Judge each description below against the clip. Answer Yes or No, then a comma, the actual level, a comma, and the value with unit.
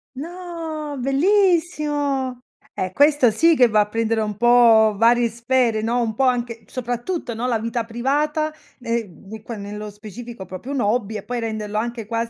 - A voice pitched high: Yes, high, 240 Hz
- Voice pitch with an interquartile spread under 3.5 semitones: No, average, 3.8 semitones